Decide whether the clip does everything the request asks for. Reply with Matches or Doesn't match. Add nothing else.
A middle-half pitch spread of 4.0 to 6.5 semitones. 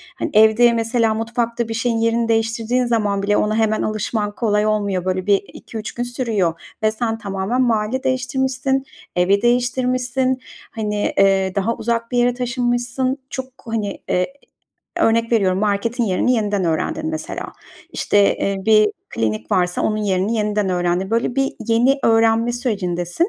Doesn't match